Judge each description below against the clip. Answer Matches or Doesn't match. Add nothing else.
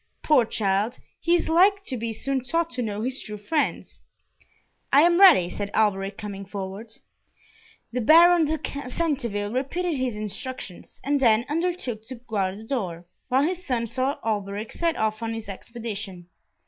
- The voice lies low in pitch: Doesn't match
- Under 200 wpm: Matches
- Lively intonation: Matches